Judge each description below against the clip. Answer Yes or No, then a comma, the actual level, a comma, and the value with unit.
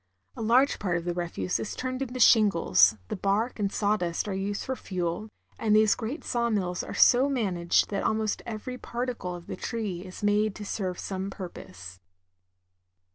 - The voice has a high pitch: Yes, high, 205 Hz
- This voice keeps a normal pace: Yes, average, 180 wpm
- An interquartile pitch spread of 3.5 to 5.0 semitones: Yes, average, 4.3 semitones